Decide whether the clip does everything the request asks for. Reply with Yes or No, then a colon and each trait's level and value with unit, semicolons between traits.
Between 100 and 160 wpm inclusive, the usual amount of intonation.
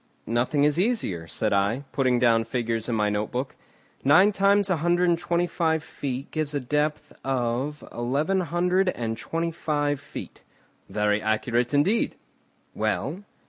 No: average, 150 wpm; wide, 6.4 semitones